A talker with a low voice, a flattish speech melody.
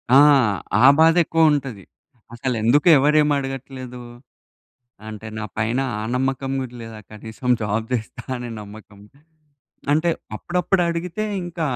No: low, 130 Hz; average, 5.3 semitones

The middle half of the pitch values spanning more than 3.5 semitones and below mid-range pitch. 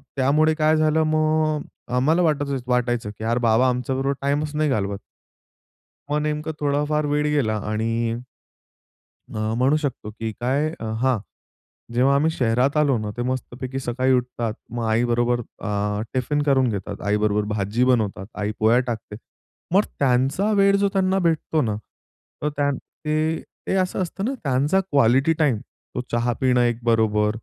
Yes: average, 4.6 semitones; low, 130 Hz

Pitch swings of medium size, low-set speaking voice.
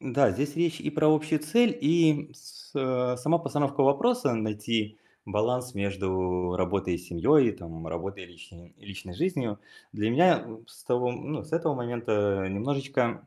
No: wide, 6.9 semitones; low, 125 Hz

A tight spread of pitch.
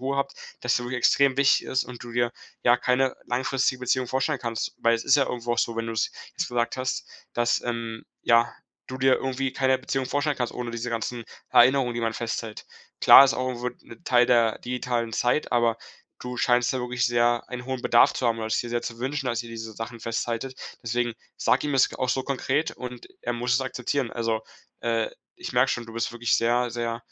Yes: narrow, 1.8 semitones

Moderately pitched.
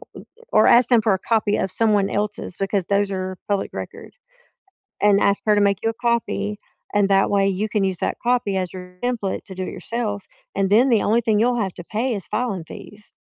No: high, 205 Hz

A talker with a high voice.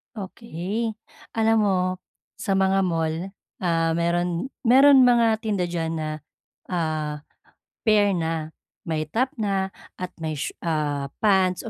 No: medium, 180 Hz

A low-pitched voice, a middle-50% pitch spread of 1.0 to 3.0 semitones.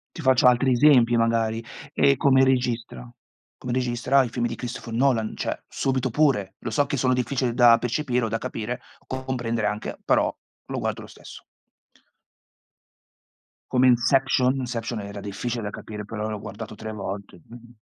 Yes: low, 120 Hz; narrow, 2.5 semitones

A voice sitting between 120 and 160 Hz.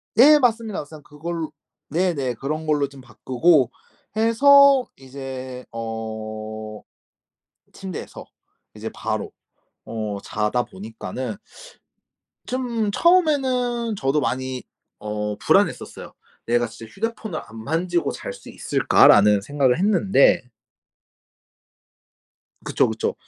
Yes: medium, 140 Hz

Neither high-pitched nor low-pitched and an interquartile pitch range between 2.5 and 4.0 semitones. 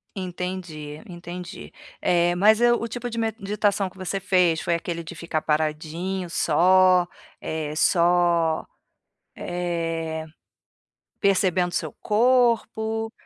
Yes: medium, 180 Hz; average, 3.1 semitones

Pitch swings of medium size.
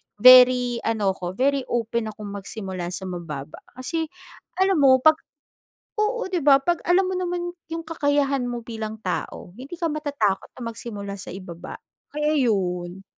No: wide, 7.4 semitones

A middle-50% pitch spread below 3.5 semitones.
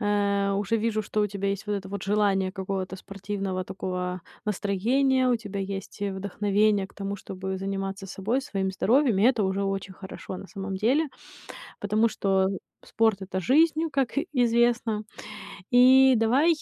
Yes: average, 2.9 semitones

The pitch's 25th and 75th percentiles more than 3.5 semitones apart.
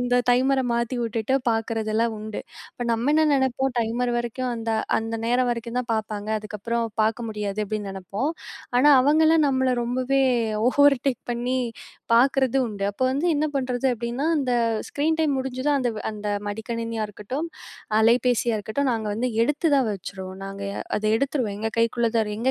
No: average, 3.2 semitones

